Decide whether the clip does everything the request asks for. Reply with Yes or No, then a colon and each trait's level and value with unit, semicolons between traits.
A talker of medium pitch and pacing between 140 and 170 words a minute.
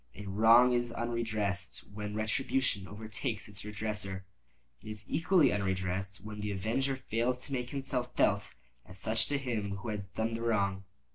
No: low, 110 Hz; average, 160 wpm